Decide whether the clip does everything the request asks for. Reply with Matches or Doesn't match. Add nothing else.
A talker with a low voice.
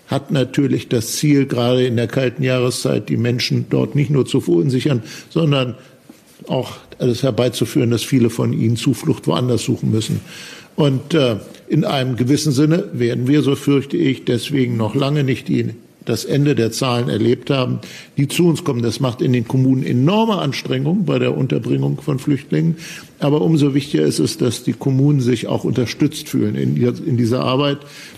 Matches